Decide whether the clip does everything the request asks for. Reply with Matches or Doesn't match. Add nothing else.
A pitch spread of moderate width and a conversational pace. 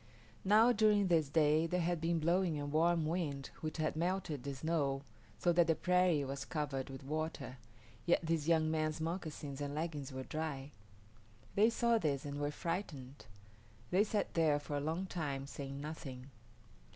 Matches